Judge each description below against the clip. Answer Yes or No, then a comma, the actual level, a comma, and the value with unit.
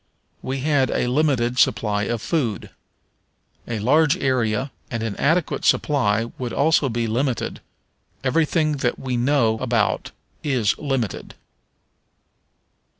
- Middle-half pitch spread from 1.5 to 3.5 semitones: No, average, 3.9 semitones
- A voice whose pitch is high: No, low, 130 Hz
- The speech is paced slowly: Yes, slow, 115 wpm